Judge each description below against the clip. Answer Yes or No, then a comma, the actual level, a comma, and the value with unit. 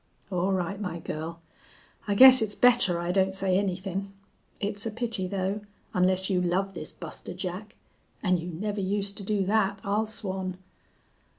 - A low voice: No, high, 195 Hz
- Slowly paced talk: No, average, 165 wpm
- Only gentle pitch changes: Yes, narrow, 2.1 semitones